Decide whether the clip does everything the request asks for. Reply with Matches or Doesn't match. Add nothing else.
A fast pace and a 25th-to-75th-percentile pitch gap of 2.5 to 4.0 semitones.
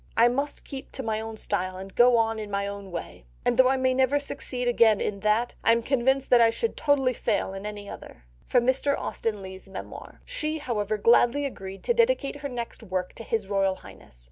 Doesn't match